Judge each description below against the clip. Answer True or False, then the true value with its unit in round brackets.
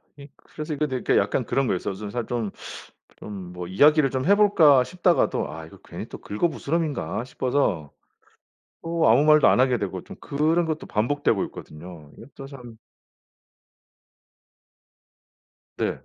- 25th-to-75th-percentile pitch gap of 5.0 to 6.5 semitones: False (6.9 semitones)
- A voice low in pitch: True (130 Hz)